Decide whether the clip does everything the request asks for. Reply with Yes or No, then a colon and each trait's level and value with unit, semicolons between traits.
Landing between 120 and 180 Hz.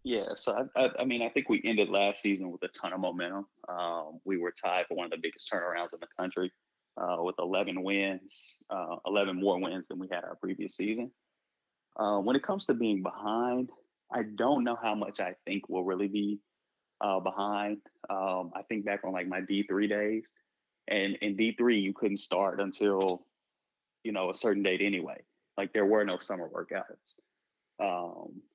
No: low, 100 Hz